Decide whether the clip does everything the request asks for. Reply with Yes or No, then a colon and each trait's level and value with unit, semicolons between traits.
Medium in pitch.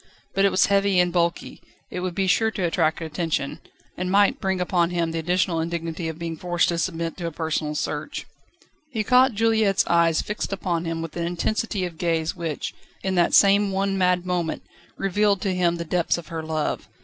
Yes: medium, 175 Hz